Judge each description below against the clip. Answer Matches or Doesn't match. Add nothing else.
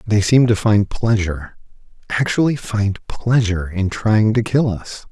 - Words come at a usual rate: Matches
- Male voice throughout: Matches